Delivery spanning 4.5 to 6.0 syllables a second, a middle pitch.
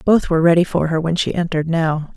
No: 6.3 syllables/s; medium, 165 Hz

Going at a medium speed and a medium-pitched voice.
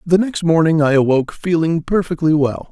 Yes: average, 175 wpm; medium, 160 Hz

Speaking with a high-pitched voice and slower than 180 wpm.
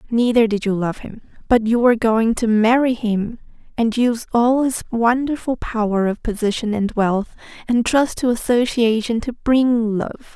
Yes: high, 230 Hz; average, 170 wpm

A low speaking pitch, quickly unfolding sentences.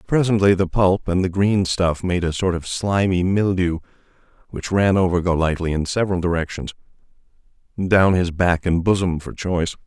No: very low, 90 Hz; average, 160 wpm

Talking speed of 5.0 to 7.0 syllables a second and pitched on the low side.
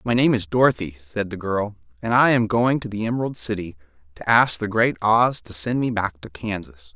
Yes: 5.3 syllables/s; low, 105 Hz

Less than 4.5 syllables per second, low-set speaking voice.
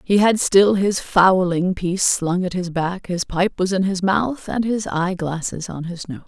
No: 4.3 syllables/s; medium, 185 Hz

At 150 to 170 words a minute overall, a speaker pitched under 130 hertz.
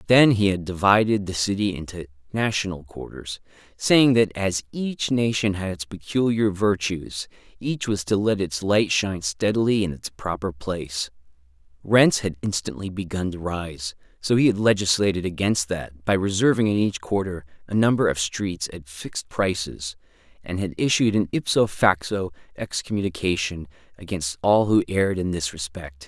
Yes: average, 155 wpm; very low, 95 Hz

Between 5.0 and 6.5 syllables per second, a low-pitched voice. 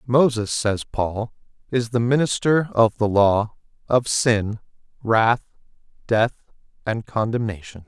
No: 3.8 syllables/s; low, 115 Hz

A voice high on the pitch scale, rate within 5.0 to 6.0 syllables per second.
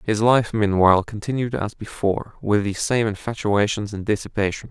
No: low, 105 Hz; 5.3 syllables/s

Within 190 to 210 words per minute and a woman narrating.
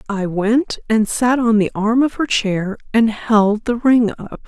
Yes: average, 200 wpm; female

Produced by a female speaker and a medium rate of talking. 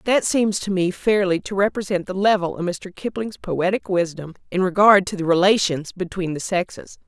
Yes: female; average, 185 wpm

